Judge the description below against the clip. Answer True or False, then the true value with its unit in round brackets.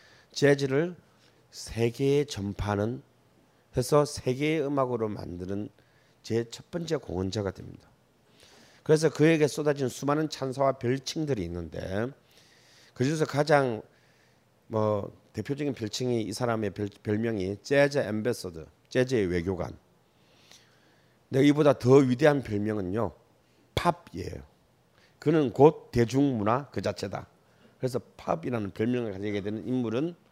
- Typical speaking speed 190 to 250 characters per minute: False (265 characters per minute)